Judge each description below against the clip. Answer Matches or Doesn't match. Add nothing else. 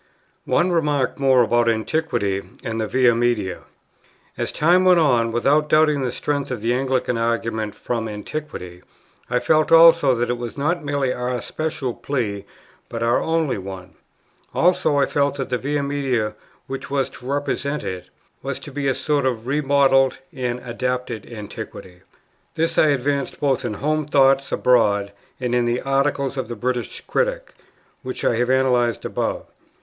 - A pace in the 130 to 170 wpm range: Matches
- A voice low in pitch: Matches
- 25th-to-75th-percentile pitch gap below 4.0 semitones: Matches